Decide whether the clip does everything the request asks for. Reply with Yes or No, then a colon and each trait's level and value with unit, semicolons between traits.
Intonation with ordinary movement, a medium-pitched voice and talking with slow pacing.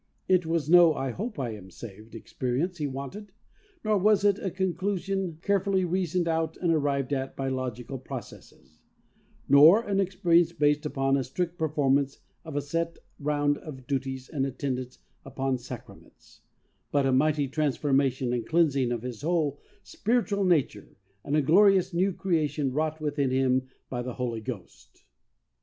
No: average, 4.8 semitones; medium, 145 Hz; average, 155 wpm